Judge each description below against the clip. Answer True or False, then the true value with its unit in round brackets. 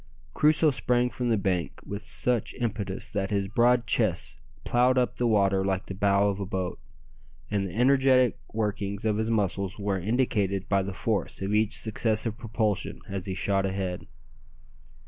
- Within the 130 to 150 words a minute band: False (165 wpm)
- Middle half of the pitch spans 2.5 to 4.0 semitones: True (3.3 semitones)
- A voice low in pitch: True (105 Hz)